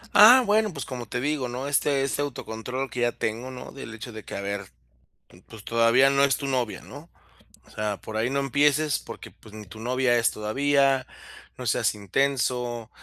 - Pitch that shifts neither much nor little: Yes, average, 3.7 semitones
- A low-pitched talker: Yes, low, 125 Hz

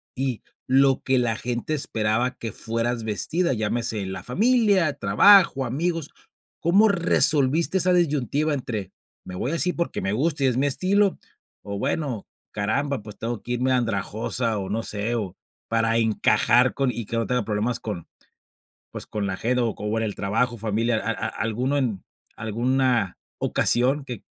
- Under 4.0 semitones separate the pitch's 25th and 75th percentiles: No, average, 4.3 semitones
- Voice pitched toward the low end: Yes, low, 120 Hz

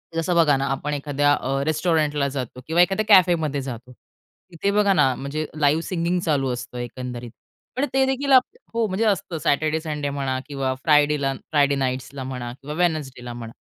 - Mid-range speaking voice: Yes, medium, 150 Hz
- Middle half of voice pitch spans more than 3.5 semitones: Yes, average, 4.1 semitones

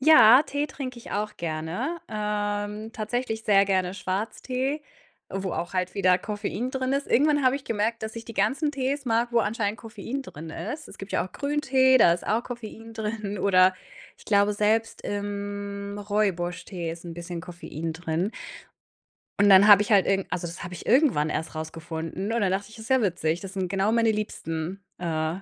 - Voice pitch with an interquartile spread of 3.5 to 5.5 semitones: Yes, average, 4.1 semitones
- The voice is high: Yes, high, 205 Hz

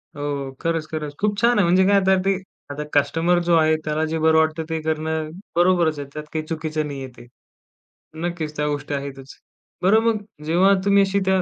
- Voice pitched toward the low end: No, medium, 160 Hz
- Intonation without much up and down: No, average, 3.3 semitones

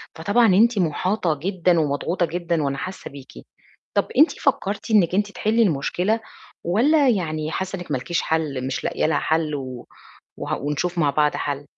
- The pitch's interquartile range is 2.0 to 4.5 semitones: No, average, 5.1 semitones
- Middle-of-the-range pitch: Yes, medium, 170 Hz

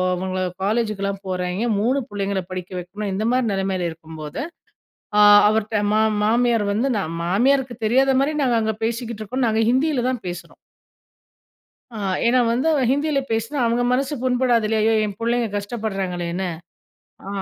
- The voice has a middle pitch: No, high, 220 Hz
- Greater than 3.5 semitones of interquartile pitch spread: Yes, average, 4.2 semitones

